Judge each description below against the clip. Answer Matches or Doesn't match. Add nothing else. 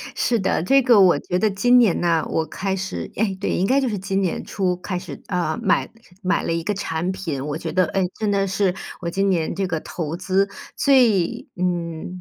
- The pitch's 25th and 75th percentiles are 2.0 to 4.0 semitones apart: Matches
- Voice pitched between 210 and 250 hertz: Doesn't match